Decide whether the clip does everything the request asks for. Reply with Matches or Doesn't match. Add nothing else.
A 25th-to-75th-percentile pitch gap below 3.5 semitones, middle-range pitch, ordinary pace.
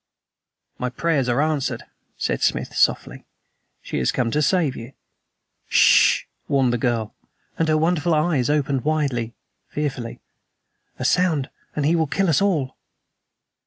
Doesn't match